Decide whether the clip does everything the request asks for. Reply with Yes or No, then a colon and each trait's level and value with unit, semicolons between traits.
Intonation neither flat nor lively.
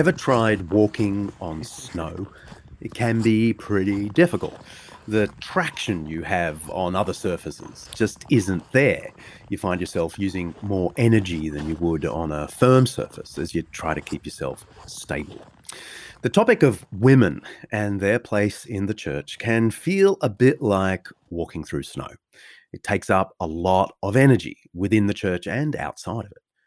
Yes: average, 4.1 semitones